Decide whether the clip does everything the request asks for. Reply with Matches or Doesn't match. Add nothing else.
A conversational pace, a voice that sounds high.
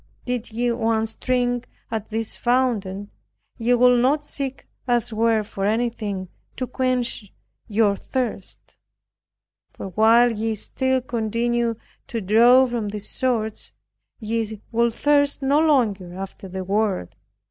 Doesn't match